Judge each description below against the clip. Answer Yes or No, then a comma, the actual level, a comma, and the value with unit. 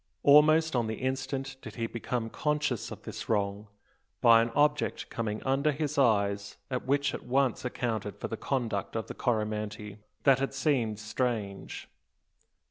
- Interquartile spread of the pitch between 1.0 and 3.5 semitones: No, average, 4.1 semitones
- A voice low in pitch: Yes, low, 120 Hz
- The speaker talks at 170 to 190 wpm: No, average, 155 wpm